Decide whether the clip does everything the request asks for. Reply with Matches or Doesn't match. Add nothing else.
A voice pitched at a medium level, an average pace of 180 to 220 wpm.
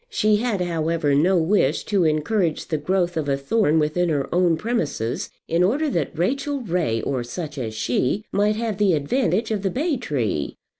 Matches